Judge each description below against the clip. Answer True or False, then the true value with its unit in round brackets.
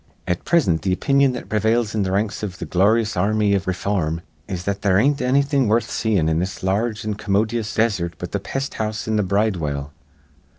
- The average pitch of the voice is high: False (105 Hz)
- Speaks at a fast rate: True (225 wpm)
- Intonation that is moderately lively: True (3.2 semitones)